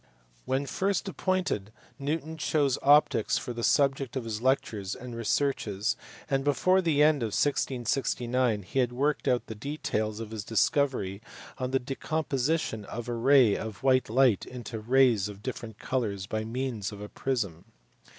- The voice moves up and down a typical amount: Yes, average, 4.1 semitones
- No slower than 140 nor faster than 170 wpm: Yes, average, 160 wpm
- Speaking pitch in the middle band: No, low, 125 Hz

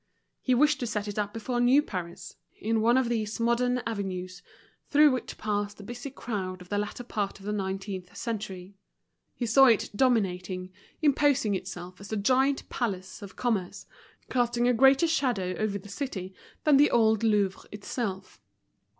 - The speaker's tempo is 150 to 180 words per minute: Yes, average, 165 wpm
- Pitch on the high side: Yes, high, 215 Hz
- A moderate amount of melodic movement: Yes, average, 4.3 semitones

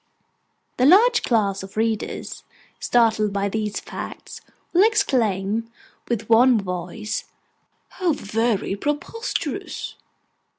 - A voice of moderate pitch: No, high, 225 Hz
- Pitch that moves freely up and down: No, average, 4.7 semitones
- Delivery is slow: Yes, slow, 95 wpm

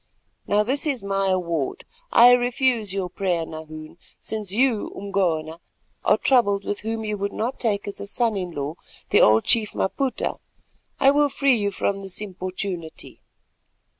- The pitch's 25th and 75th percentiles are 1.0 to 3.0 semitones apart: No, average, 4.3 semitones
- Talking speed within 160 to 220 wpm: Yes, average, 165 wpm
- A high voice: Yes, high, 200 Hz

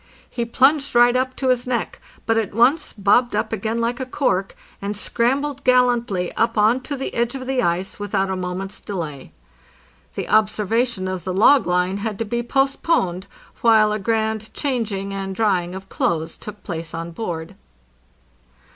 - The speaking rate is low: No, average, 175 wpm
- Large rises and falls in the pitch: No, average, 4.2 semitones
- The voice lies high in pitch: Yes, high, 220 Hz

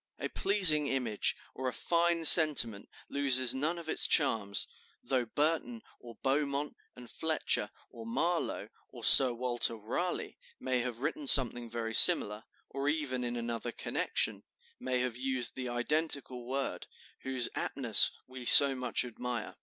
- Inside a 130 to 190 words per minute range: Yes, average, 145 wpm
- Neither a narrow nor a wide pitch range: Yes, average, 3.6 semitones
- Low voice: Yes, low, 130 Hz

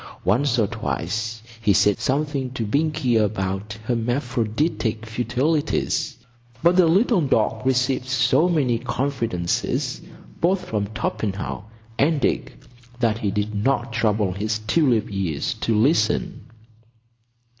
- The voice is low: Yes, low, 115 Hz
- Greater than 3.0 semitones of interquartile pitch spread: Yes, average, 4.3 semitones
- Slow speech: Yes, slow, 115 wpm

